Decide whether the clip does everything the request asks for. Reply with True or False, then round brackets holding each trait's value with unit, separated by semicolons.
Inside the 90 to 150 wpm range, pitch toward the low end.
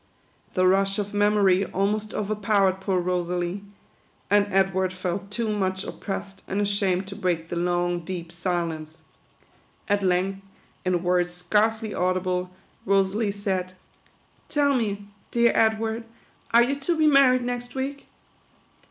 False (140 wpm; 195 Hz)